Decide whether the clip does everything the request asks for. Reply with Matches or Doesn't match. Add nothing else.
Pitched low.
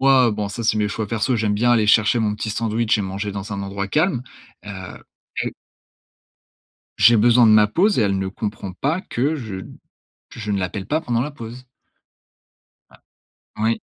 Matches